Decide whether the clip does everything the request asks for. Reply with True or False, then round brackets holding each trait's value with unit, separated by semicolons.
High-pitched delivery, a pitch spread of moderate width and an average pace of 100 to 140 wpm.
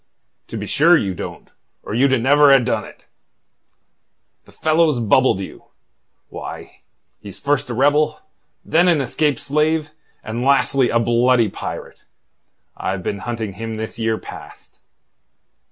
False (125 Hz; 4.6 semitones; 135 wpm)